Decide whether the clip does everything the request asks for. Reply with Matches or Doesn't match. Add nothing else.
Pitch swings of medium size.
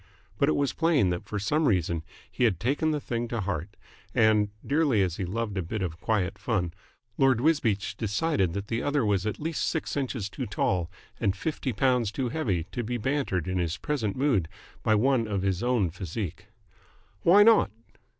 Doesn't match